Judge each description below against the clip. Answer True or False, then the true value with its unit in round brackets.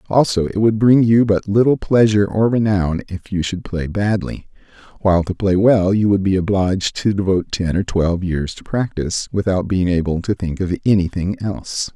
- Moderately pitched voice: False (100 Hz)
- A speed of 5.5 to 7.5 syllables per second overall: False (5.3 syllables/s)